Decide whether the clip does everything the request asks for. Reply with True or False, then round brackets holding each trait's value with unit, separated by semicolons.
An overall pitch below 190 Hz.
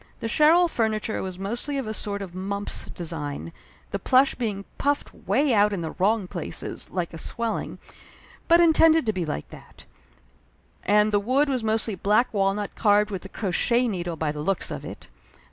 False (210 Hz)